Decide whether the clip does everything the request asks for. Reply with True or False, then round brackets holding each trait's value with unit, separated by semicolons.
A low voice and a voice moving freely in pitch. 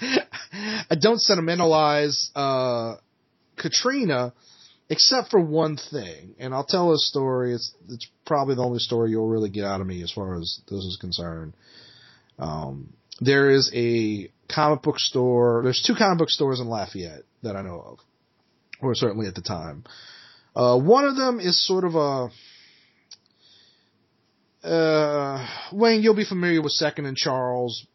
True (130 Hz; 6.2 semitones)